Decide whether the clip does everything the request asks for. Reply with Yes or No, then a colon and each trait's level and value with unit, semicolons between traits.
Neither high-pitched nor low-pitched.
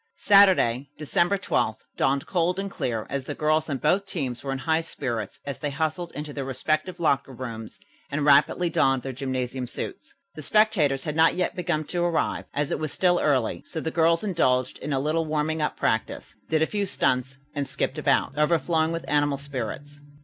Yes: medium, 150 Hz